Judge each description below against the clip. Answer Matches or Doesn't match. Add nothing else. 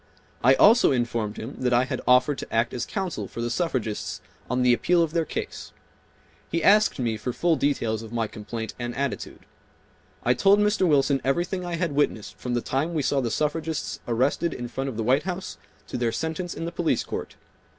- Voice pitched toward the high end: Doesn't match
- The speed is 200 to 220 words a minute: Matches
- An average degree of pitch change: Doesn't match